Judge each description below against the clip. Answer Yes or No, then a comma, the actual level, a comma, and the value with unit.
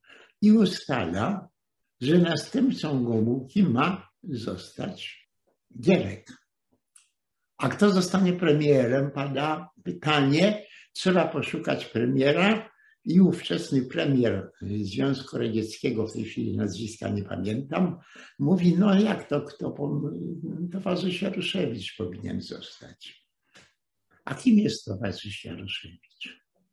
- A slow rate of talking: Yes, slow, 95 wpm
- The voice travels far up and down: Yes, wide, 8.2 semitones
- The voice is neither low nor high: Yes, medium, 145 Hz